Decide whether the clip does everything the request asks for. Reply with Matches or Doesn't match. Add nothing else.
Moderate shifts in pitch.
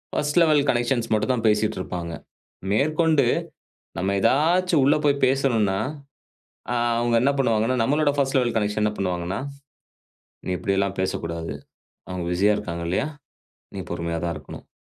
Doesn't match